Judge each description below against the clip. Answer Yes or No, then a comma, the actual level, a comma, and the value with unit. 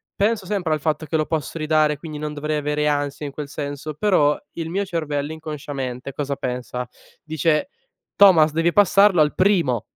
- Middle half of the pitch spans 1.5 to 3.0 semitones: Yes, narrow, 2.4 semitones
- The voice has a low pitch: No, medium, 155 Hz